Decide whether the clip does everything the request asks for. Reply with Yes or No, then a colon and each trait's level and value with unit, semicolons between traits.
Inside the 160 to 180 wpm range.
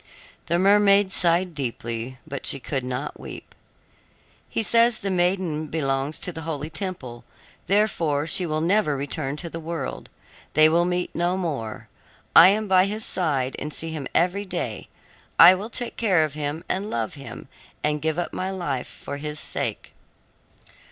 Yes: average, 165 wpm